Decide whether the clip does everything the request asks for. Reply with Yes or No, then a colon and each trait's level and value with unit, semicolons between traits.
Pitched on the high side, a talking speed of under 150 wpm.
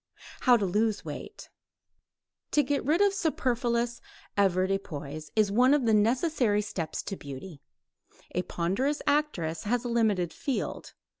Yes: high, 220 Hz; slow, 135 wpm